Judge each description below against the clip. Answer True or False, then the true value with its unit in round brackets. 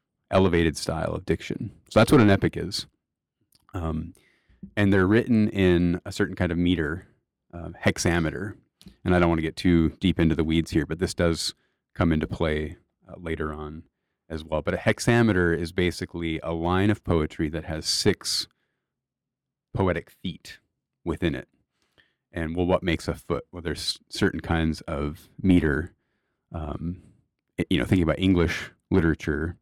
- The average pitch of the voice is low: True (85 Hz)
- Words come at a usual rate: True (160 wpm)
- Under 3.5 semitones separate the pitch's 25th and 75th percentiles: True (2.6 semitones)